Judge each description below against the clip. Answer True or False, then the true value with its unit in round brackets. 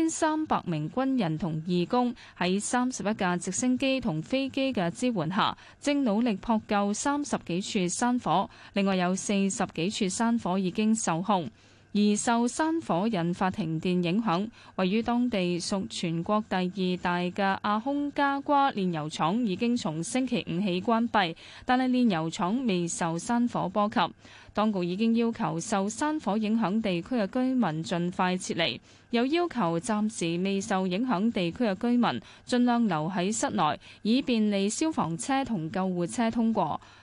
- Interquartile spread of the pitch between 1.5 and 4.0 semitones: False (5.0 semitones)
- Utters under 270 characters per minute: True (240 characters per minute)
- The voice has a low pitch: False (205 Hz)